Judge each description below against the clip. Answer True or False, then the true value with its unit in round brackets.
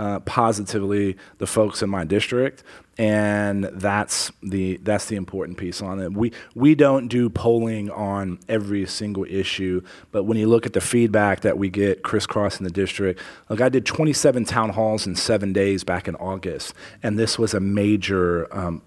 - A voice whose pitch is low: True (100 Hz)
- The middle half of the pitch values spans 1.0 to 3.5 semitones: True (2.6 semitones)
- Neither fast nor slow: True (180 wpm)